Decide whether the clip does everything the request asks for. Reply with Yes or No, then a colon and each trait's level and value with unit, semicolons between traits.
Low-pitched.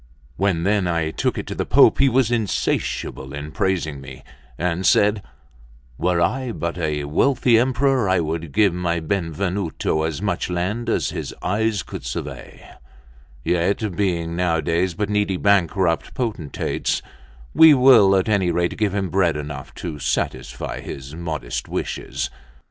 Yes: very low, 90 Hz